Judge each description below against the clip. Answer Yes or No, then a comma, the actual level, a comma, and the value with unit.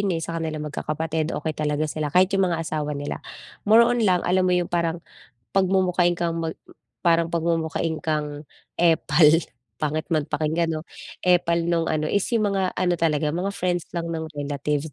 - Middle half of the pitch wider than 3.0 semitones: No, narrow, 2.4 semitones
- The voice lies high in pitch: No, medium, 165 Hz